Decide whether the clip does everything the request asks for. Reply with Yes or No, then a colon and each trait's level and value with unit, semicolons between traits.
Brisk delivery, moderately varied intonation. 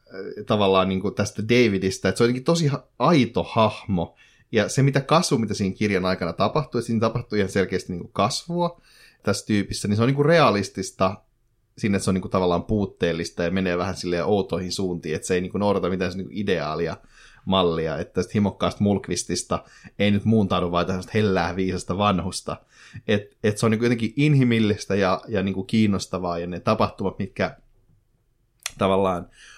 Yes: fast, 175 wpm; average, 3.5 semitones